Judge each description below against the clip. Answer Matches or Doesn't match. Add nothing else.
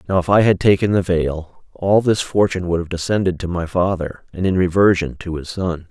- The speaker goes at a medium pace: Doesn't match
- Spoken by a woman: Doesn't match